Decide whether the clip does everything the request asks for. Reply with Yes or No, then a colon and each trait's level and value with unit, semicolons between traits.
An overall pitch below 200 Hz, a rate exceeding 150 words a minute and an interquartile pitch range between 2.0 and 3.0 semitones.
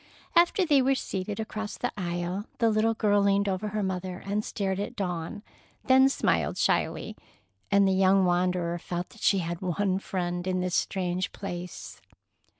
Yes: high, 190 Hz; average, 165 wpm; narrow, 2.5 semitones